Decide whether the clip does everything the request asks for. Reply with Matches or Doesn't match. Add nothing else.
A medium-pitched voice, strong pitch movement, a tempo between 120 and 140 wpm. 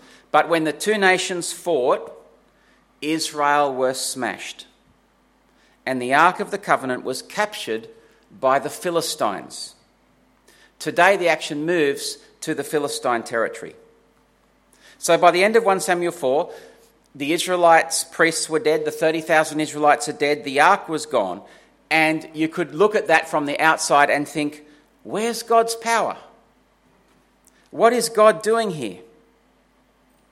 Matches